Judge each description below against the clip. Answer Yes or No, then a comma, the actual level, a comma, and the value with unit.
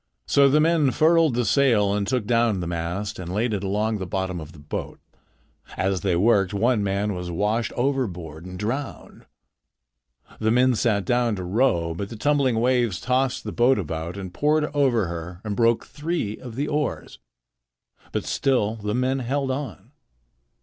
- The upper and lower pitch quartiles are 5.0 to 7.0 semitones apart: Yes, wide, 5.4 semitones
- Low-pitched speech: Yes, low, 110 Hz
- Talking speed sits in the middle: Yes, average, 175 wpm